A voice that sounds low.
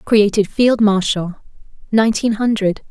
No: high, 210 Hz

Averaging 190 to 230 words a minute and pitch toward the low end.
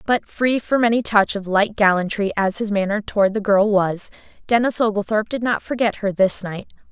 No: average, 200 wpm; high, 210 Hz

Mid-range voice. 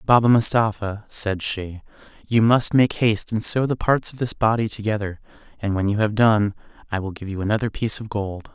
No: low, 105 Hz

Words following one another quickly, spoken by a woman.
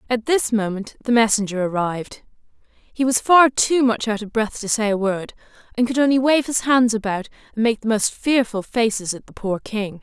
Yes: fast, 210 wpm; female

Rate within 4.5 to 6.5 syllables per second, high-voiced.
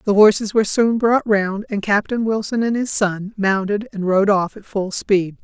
Yes: 4.7 syllables/s; high, 205 Hz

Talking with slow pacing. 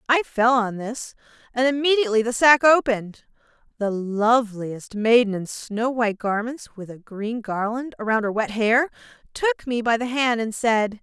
No: average, 170 wpm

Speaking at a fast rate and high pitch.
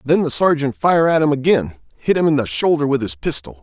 No: fast, 250 wpm; low, 135 Hz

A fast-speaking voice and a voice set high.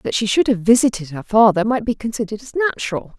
Yes: fast, 225 wpm; high, 220 Hz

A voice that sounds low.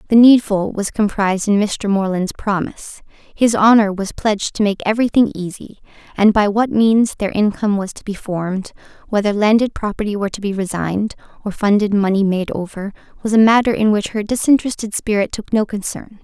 No: high, 205 Hz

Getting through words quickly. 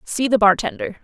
No: average, 175 wpm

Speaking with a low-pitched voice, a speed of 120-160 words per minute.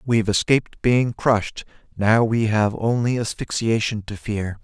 Yes: low, 110 Hz; average, 140 wpm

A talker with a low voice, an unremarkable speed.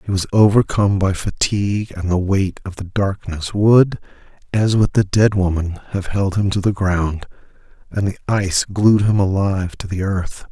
Yes: very low, 95 Hz; average, 185 wpm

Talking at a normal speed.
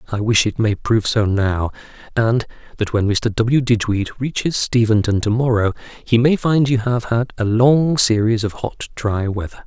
Yes: average, 185 wpm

